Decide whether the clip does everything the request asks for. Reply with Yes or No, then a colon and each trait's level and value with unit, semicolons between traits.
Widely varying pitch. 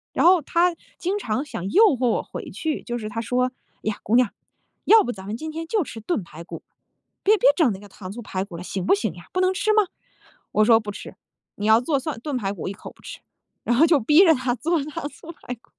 Yes: wide, 7.6 semitones